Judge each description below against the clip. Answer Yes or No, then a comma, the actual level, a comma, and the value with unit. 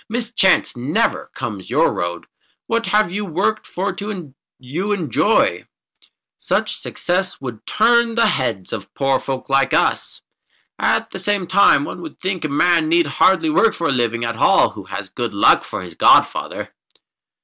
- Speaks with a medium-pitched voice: Yes, medium, 165 Hz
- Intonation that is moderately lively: No, wide, 8.8 semitones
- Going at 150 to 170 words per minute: Yes, average, 160 wpm